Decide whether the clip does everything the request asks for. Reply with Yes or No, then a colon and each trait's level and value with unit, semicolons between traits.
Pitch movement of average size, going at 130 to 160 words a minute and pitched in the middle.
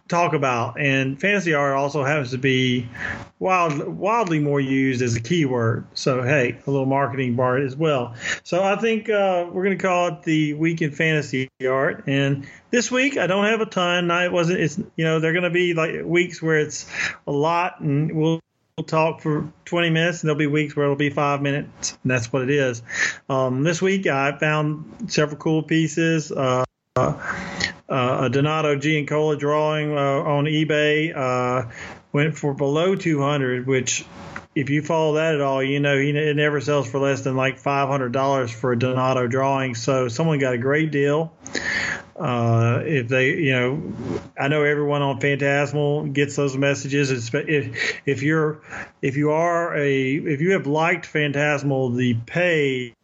No: average, 3.0 semitones; average, 180 wpm; medium, 145 Hz